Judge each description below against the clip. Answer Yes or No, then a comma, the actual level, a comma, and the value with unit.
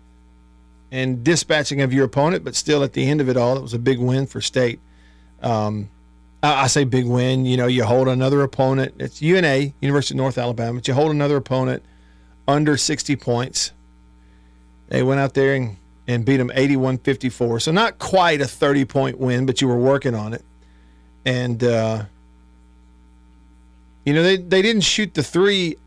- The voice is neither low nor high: No, low, 130 Hz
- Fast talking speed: No, average, 180 wpm